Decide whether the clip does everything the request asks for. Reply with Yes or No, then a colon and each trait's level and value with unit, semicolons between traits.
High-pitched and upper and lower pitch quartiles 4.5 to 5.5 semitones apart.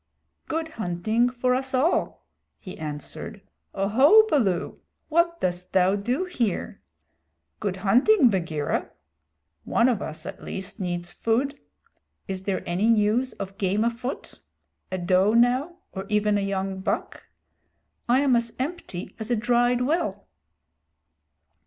Yes: high, 220 Hz; average, 5.0 semitones